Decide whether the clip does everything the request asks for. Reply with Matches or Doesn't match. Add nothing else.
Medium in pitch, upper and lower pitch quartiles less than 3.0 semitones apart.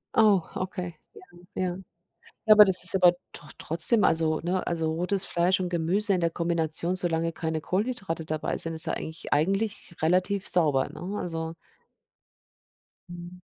Matches